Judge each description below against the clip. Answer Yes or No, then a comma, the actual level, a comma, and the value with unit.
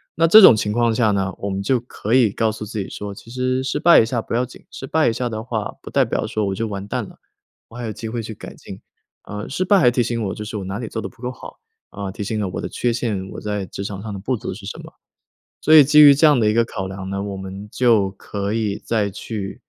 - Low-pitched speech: Yes, low, 110 Hz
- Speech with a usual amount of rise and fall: Yes, average, 3.4 semitones